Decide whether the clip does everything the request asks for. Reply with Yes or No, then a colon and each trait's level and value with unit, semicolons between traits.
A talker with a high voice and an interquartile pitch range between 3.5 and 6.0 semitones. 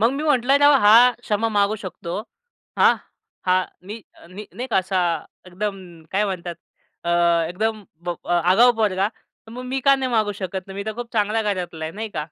Yes: high, 210 Hz; average, 3.9 semitones